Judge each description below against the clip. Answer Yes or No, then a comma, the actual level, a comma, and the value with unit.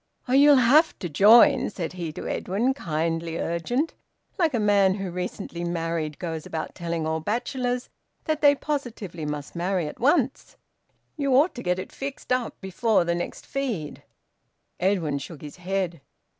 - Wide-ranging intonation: Yes, wide, 7.1 semitones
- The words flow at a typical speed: Yes, average, 160 wpm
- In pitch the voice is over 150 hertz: Yes, high, 190 Hz